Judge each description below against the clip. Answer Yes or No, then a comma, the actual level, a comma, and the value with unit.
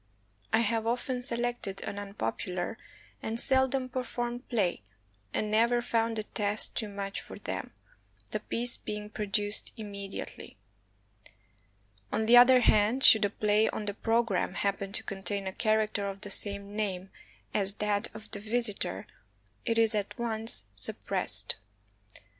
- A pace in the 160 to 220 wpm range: No, average, 145 wpm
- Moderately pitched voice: No, high, 215 Hz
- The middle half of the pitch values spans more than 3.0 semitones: No, narrow, 2.6 semitones